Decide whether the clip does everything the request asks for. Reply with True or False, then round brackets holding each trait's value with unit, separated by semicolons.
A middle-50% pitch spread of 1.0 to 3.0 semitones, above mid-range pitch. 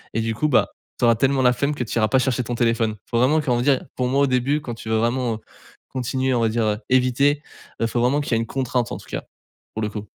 False (2.6 semitones; 125 Hz)